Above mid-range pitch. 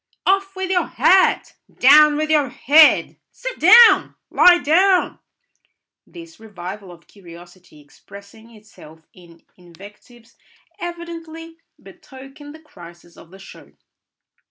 Yes: very high, 265 Hz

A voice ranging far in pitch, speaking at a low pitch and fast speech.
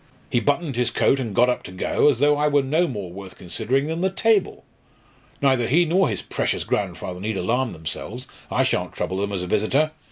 Yes: wide, 6.5 semitones; low, 125 Hz; fast, 215 wpm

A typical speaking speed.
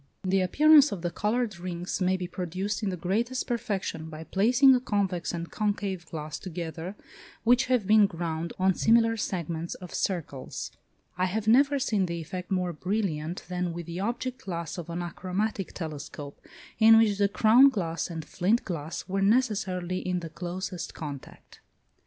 Yes: average, 165 wpm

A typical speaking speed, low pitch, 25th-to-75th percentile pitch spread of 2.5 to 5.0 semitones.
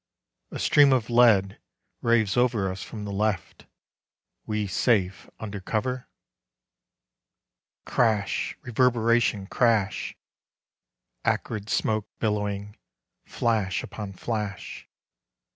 No: slow, 90 wpm; low, 110 Hz; average, 2.8 semitones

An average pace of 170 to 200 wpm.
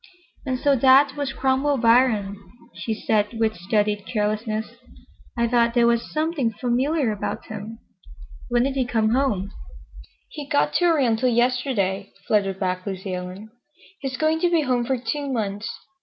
No: average, 155 wpm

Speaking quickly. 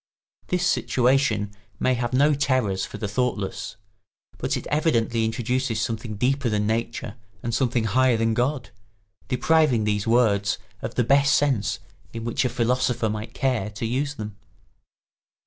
No: average, 145 wpm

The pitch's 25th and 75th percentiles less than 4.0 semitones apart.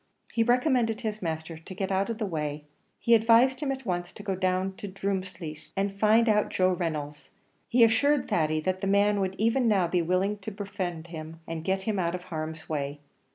No: average, 4.4 semitones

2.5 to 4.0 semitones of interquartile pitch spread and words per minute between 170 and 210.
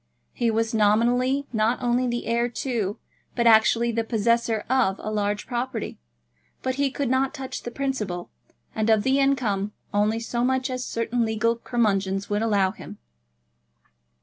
No: average, 2.9 semitones; average, 155 wpm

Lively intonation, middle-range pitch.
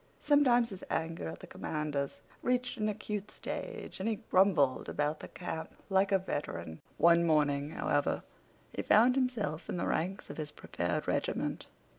Yes: wide, 6.2 semitones; medium, 175 Hz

